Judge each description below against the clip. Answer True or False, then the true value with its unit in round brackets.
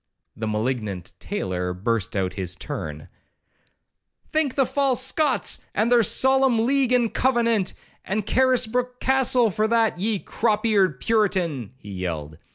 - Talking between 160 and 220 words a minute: False (140 wpm)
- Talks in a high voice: True (215 Hz)